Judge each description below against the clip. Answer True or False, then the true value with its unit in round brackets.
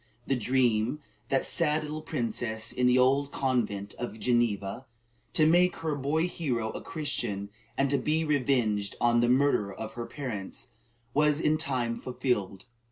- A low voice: True (125 Hz)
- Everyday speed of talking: True (160 wpm)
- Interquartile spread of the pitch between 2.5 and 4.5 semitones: False (4.9 semitones)